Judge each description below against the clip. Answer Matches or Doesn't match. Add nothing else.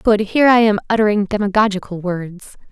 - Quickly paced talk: Doesn't match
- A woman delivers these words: Matches